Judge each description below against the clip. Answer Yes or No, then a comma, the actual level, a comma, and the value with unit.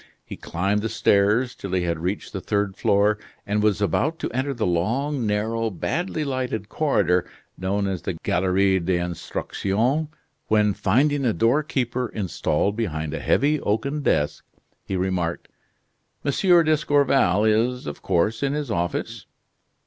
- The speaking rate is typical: Yes, average, 145 wpm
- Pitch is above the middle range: No, low, 105 Hz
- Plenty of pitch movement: Yes, wide, 5.8 semitones